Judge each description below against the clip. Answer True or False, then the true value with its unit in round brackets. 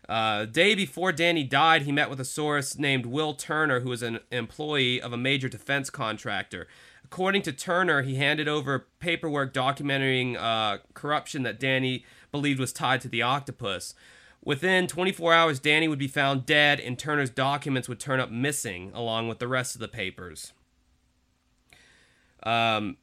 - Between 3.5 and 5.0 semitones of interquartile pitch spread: True (3.8 semitones)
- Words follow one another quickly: False (165 wpm)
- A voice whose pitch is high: False (135 Hz)